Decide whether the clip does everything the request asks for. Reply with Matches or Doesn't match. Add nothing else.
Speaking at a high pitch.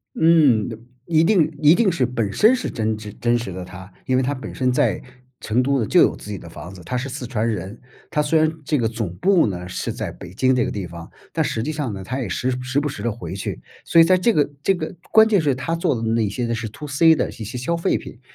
Doesn't match